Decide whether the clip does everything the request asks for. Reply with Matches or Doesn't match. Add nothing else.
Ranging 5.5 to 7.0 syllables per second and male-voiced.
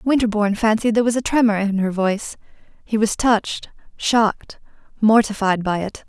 Doesn't match